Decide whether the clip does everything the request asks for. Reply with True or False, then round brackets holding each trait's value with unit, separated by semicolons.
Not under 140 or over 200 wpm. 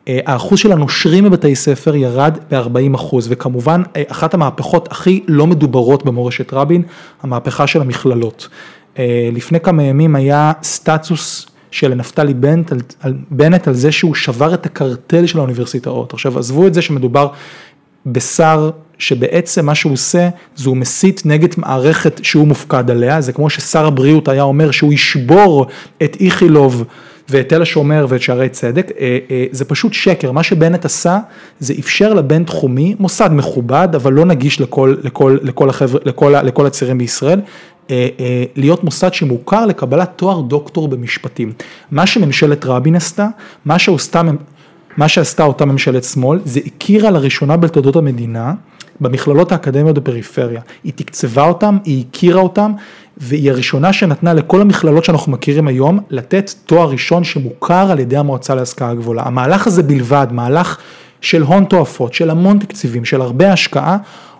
True (145 wpm)